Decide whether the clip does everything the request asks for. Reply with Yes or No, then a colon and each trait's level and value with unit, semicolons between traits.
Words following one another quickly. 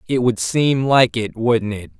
Yes: fast, 210 wpm